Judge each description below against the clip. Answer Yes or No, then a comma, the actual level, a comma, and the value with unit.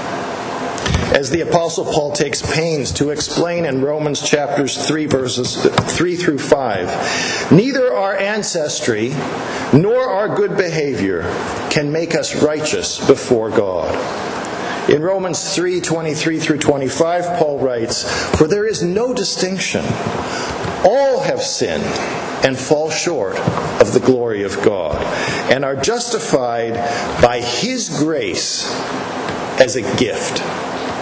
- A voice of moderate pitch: Yes, medium, 160 Hz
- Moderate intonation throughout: Yes, average, 4.9 semitones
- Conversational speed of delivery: No, slow, 120 wpm